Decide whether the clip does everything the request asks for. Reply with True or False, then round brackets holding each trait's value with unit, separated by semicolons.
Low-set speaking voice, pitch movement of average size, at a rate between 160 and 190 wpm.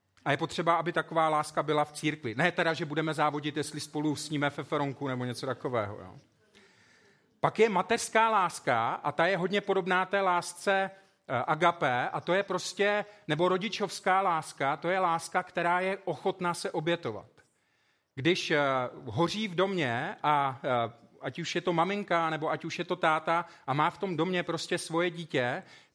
False (165 Hz; 3.5 semitones; 170 wpm)